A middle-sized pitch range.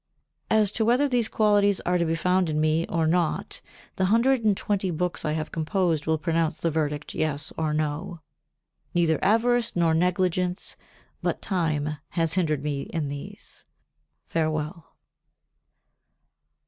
Yes: average, 3.5 semitones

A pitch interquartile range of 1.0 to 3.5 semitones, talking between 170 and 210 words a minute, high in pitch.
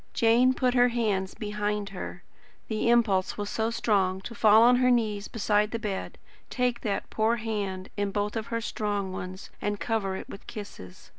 Yes: narrow, 2.5 semitones; average, 175 wpm; high, 210 Hz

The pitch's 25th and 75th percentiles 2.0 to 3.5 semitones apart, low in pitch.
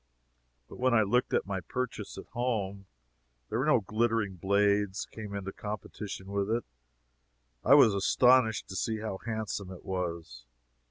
Yes: average, 2.9 semitones; low, 105 Hz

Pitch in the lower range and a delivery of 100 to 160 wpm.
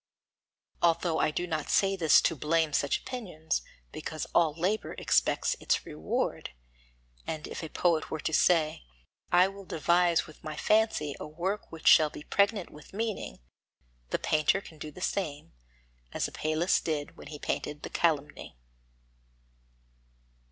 No: medium, 160 Hz; average, 150 wpm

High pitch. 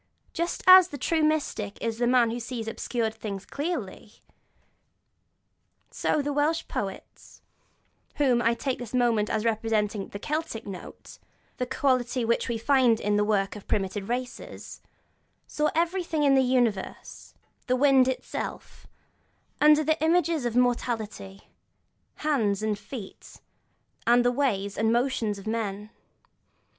Yes: high, 240 Hz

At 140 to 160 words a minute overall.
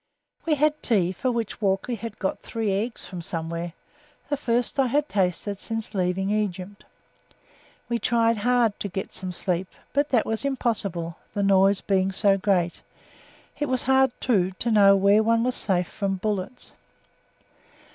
Yes: average, 155 wpm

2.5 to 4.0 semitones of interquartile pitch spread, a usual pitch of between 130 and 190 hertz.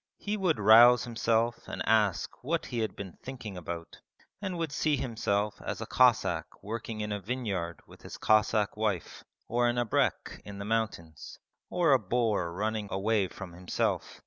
No: average, 3.5 semitones; low, 110 Hz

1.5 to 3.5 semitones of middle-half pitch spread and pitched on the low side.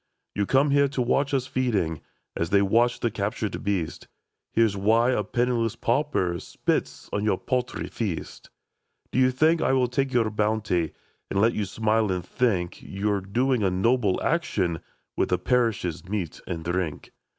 No: average, 4.6 semitones; low, 110 Hz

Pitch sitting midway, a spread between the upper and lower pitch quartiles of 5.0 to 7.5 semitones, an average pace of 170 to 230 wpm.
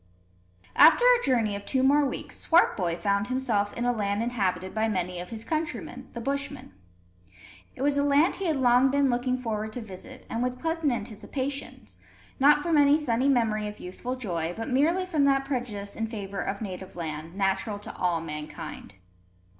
No: high, 235 Hz; wide, 5.6 semitones; average, 180 wpm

